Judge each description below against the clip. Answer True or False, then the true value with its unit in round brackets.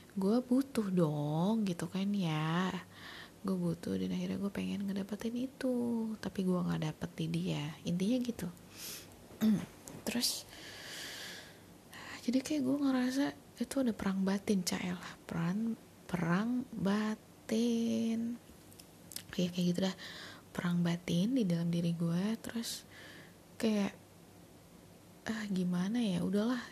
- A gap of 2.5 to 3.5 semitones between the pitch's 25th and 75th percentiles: False (4.9 semitones)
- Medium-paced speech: True (115 wpm)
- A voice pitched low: False (195 Hz)